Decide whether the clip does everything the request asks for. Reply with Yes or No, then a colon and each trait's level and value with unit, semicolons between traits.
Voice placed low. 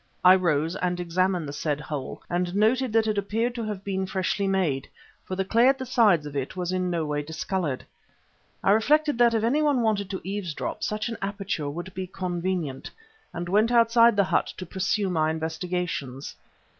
No: medium, 185 Hz